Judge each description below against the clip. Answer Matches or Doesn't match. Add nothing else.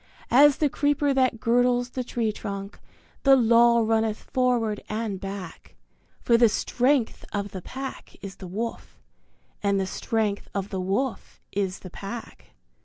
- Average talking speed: Matches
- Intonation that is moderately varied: Matches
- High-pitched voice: Matches